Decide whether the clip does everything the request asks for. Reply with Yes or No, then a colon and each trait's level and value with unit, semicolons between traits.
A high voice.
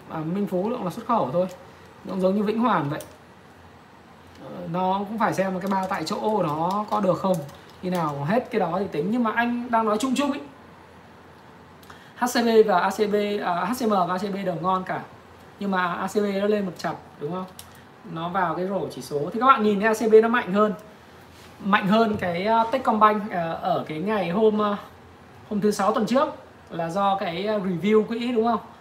Yes: high, 205 Hz